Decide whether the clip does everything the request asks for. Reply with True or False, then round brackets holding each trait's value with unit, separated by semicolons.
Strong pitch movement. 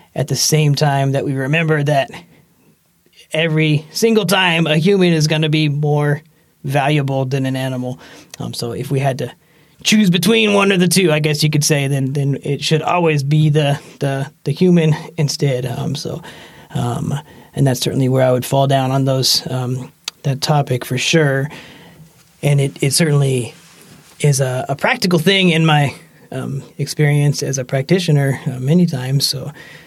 False (2.8 semitones)